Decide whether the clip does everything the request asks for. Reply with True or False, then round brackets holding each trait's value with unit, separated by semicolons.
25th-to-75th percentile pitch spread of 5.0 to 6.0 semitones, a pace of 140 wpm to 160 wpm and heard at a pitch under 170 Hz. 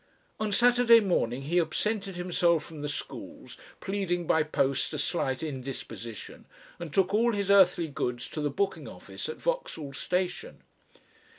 False (5.5 semitones; 150 wpm; 175 Hz)